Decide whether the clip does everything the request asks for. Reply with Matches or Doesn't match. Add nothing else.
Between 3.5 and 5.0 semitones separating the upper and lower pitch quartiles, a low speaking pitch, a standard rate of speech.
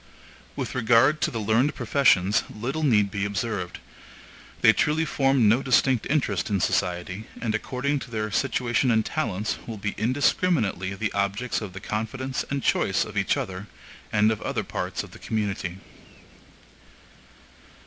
Matches